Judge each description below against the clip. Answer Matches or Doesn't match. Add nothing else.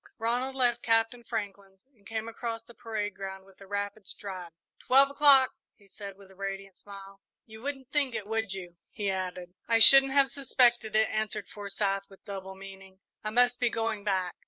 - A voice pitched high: Matches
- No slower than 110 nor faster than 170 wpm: Doesn't match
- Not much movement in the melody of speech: Doesn't match